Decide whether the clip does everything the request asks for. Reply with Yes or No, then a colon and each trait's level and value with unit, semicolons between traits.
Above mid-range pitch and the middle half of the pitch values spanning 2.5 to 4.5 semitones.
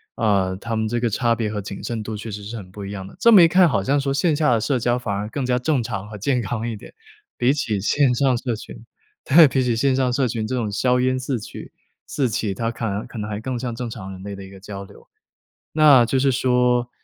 No: low, 120 Hz; average, 3.7 semitones